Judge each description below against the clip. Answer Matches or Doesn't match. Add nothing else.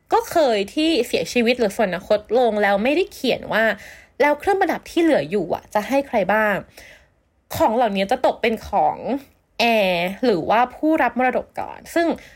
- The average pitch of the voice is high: Matches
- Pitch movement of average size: Doesn't match